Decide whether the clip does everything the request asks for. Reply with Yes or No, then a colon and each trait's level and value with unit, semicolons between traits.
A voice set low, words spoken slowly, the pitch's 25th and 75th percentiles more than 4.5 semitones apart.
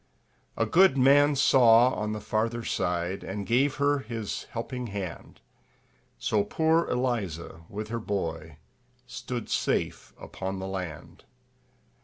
Yes: low, 110 Hz; slow, 125 wpm; average, 5.1 semitones